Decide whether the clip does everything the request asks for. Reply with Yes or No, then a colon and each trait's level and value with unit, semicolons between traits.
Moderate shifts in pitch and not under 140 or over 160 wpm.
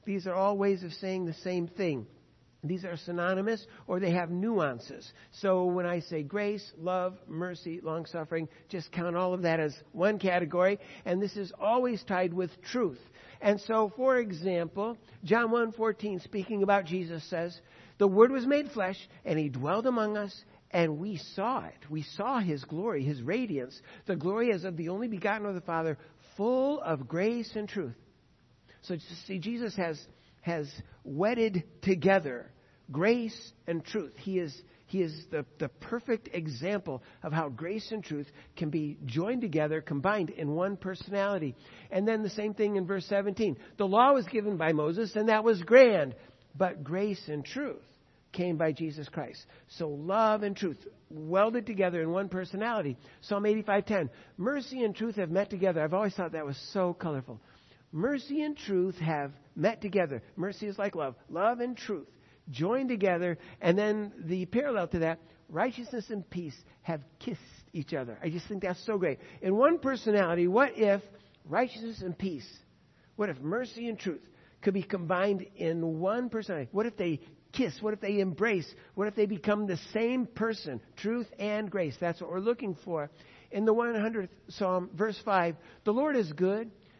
No: average, 4.3 semitones; average, 175 wpm